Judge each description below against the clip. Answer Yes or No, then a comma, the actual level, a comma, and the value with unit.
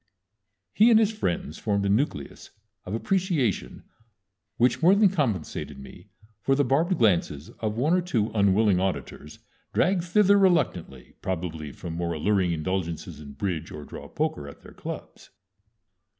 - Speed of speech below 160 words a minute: Yes, average, 150 wpm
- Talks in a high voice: No, low, 100 Hz